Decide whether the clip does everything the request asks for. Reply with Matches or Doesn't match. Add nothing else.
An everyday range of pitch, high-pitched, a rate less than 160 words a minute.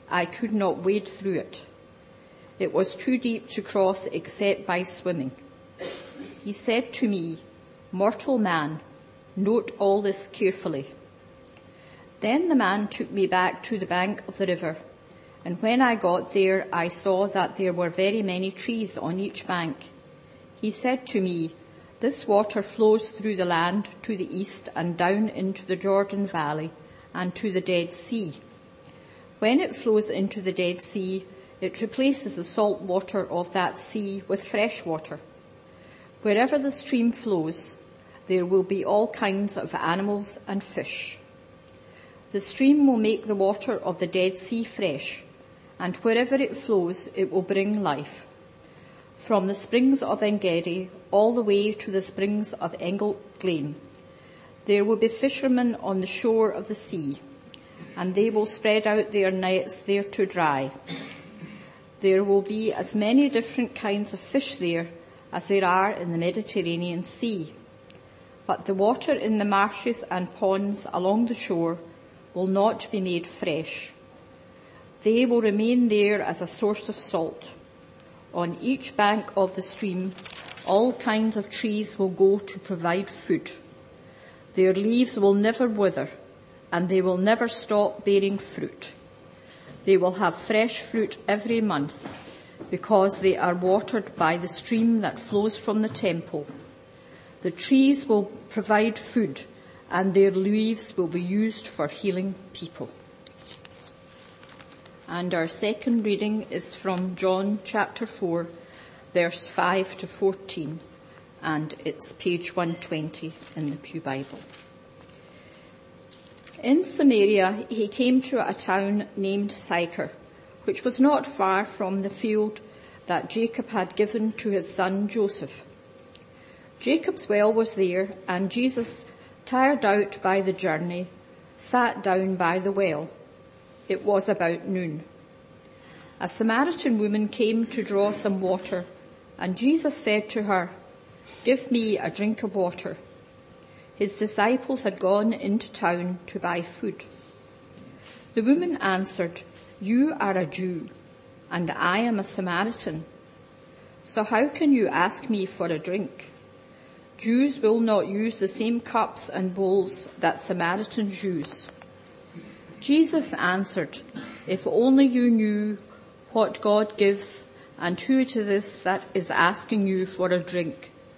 Matches